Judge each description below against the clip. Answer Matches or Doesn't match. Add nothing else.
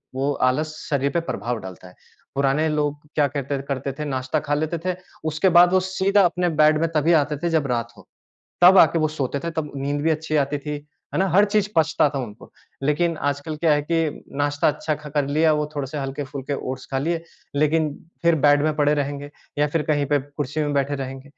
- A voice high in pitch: Doesn't match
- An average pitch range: Doesn't match